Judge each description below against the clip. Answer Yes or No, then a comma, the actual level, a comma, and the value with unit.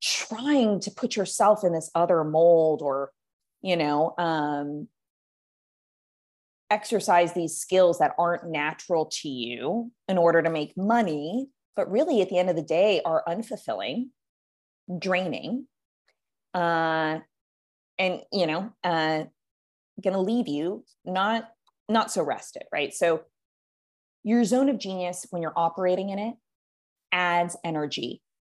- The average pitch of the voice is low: No, medium, 180 Hz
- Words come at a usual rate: No, slow, 130 wpm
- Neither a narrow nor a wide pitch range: Yes, average, 4.9 semitones